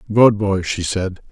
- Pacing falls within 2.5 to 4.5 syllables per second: Yes, 4.2 syllables/s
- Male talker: Yes, male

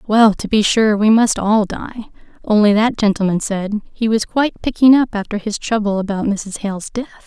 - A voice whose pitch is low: No, high, 215 Hz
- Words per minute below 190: No, average, 200 wpm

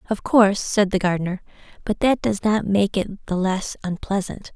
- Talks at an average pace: Yes, average, 185 wpm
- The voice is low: No, high, 200 Hz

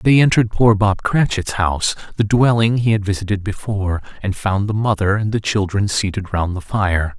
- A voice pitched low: Yes, low, 100 Hz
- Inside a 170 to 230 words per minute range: Yes, average, 190 wpm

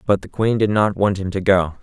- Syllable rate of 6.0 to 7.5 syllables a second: No, 5.3 syllables/s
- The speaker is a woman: No, male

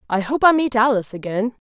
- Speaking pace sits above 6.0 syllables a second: Yes, 6.4 syllables/s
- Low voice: No, high, 235 Hz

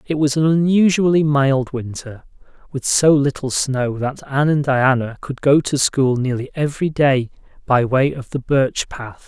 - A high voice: No, medium, 140 Hz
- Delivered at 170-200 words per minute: Yes, average, 175 wpm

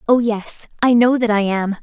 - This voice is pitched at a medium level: No, high, 225 Hz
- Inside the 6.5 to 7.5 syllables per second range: No, 4.6 syllables/s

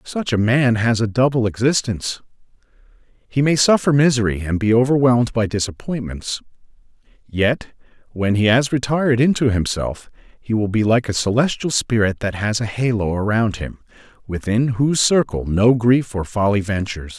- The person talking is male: Yes, male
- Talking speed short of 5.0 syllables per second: No, 5.1 syllables/s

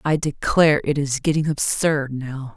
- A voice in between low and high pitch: Yes, medium, 145 Hz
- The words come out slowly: No, average, 165 wpm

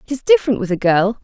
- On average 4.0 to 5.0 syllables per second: No, 7.3 syllables/s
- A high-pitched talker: Yes, high, 230 Hz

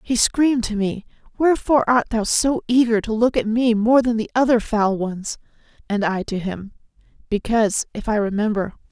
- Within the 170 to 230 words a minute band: Yes, average, 180 wpm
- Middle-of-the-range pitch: No, high, 225 Hz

